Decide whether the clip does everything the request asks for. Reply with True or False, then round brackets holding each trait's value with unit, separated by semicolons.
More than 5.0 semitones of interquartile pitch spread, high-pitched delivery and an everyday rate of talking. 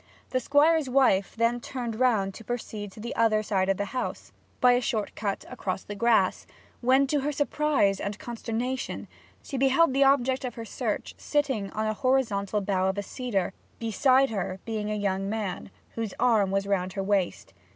False (4.4 semitones; 225 Hz; 185 wpm)